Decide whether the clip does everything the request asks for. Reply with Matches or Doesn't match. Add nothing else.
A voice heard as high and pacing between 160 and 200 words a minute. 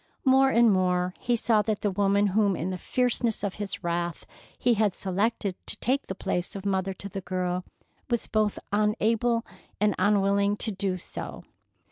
Matches